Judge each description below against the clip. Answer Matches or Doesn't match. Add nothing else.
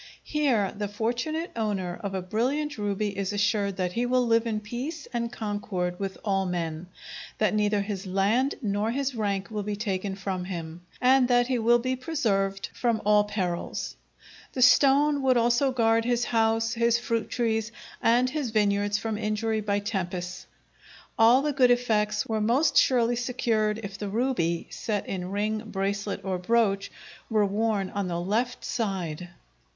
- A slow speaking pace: Doesn't match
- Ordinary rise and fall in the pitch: Matches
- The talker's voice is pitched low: Doesn't match